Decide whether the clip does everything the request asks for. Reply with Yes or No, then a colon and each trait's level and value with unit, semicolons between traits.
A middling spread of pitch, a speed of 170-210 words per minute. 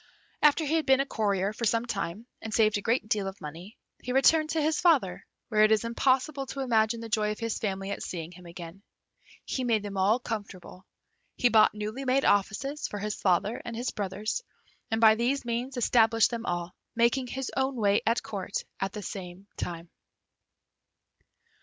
Yes: average, 4.0 semitones; average, 190 wpm